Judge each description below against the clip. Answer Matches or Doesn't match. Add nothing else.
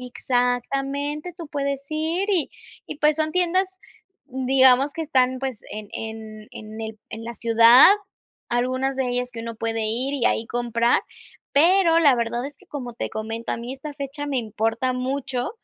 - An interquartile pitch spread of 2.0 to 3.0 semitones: Doesn't match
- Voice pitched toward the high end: Matches